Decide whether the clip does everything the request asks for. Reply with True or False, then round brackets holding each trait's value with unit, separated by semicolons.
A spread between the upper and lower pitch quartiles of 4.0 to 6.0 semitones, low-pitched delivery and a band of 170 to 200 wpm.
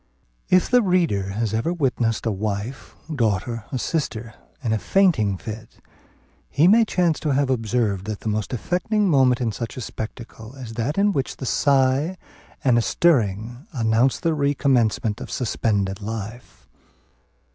False (4.7 semitones; 120 Hz; 155 wpm)